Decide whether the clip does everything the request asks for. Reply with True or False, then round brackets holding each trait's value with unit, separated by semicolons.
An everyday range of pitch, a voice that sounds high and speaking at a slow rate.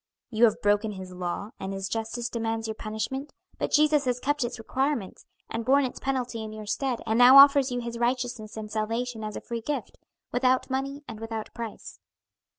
False (3.1 semitones; 235 Hz; 195 wpm)